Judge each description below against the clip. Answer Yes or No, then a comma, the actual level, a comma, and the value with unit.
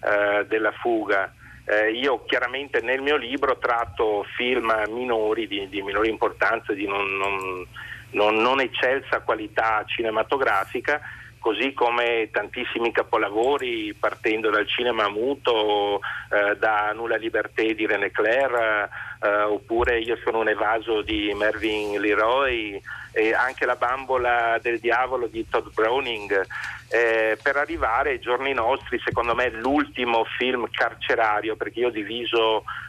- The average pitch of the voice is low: Yes, low, 115 Hz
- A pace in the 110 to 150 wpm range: Yes, average, 130 wpm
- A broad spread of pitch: No, average, 3.8 semitones